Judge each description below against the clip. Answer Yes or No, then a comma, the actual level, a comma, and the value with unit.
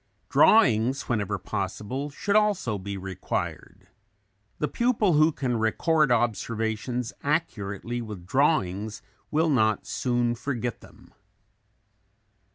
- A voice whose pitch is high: No, low, 120 Hz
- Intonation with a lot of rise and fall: Yes, wide, 5.7 semitones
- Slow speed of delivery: Yes, slow, 100 wpm